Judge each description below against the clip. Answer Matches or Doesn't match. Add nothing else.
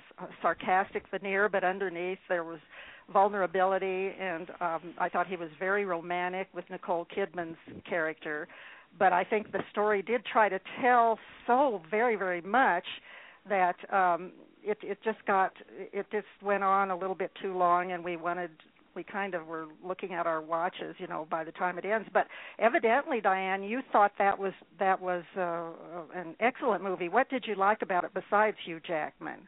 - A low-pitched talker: Doesn't match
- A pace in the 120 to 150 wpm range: Doesn't match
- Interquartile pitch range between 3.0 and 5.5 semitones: Doesn't match